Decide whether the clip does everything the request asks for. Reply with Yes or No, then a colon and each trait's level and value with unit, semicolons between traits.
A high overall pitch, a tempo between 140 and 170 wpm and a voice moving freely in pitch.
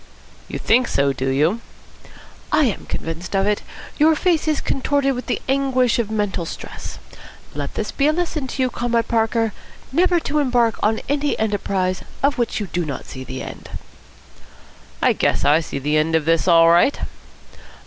No: high, 220 Hz; average, 180 wpm; wide, 8.4 semitones